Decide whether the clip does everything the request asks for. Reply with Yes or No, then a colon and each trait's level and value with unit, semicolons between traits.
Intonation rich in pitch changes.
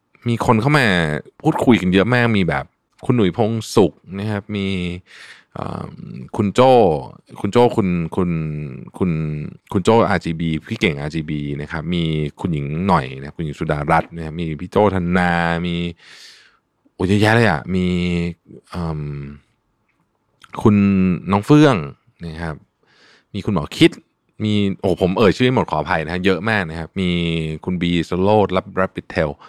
No: average, 3.8 semitones